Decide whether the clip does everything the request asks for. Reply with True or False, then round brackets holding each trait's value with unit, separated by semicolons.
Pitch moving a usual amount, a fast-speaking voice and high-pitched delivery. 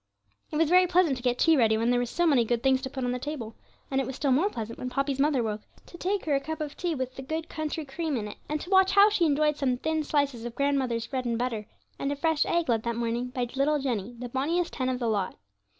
True (4.3 semitones; 280 wpm; 270 Hz)